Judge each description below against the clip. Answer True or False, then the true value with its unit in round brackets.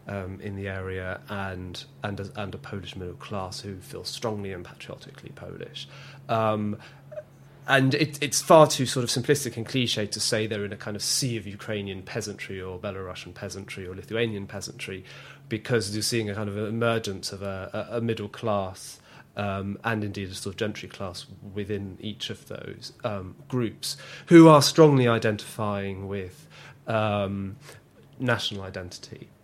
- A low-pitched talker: True (105 Hz)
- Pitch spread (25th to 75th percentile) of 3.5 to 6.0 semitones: True (4.2 semitones)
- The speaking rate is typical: True (165 wpm)